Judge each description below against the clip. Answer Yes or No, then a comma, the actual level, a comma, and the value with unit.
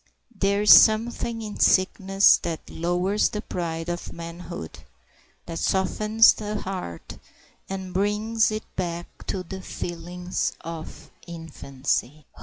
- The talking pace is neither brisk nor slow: No, slow, 115 wpm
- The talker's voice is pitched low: No, medium, 185 Hz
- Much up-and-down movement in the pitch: No, average, 3.7 semitones